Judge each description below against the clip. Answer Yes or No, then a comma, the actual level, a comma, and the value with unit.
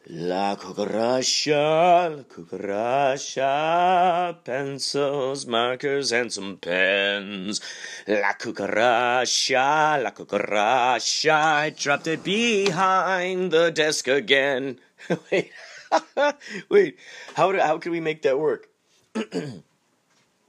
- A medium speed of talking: No, slow, 90 wpm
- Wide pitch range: Yes, wide, 5.7 semitones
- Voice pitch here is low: No, medium, 155 Hz